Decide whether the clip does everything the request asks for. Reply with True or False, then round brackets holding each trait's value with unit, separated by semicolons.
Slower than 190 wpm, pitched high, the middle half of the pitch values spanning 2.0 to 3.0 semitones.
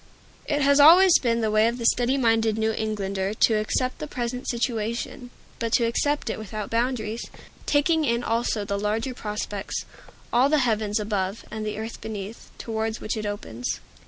True (175 wpm; 225 Hz; 2.5 semitones)